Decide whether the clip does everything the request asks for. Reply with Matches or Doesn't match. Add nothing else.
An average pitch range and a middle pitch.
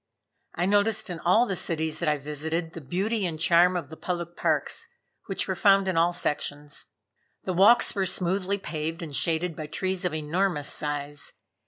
Matches